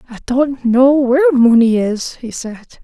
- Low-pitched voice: No, very high, 250 Hz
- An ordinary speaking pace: Yes, average, 170 wpm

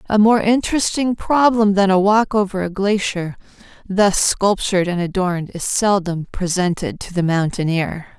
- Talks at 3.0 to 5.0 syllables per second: Yes, 4.7 syllables/s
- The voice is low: No, high, 195 Hz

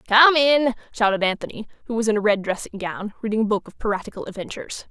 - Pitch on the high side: Yes, high, 220 Hz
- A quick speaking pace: Yes, fast, 210 wpm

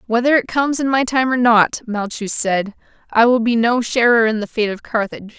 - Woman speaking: Yes, female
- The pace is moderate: No, fast, 225 wpm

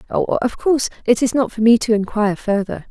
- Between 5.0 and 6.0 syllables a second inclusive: Yes, 5.6 syllables/s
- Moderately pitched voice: No, high, 230 Hz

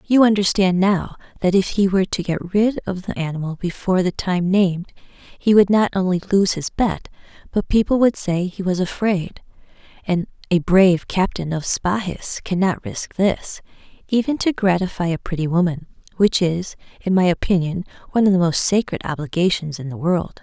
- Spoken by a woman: Yes, female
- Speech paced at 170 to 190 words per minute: Yes, average, 175 wpm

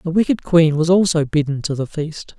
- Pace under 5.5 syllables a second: Yes, 5.1 syllables/s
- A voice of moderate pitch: Yes, medium, 160 Hz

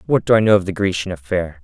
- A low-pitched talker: Yes, very low, 90 Hz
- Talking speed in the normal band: No, fast, 295 wpm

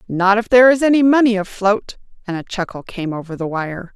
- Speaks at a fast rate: Yes, fast, 210 wpm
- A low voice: No, high, 205 Hz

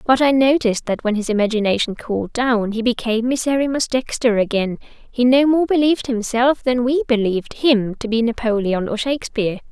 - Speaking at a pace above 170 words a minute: No, average, 165 wpm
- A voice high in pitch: Yes, high, 235 Hz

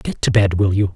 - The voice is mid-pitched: No, very low, 95 Hz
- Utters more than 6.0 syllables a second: No, 5.6 syllables/s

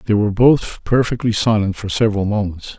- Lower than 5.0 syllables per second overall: No, 5.8 syllables/s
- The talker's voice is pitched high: No, low, 105 Hz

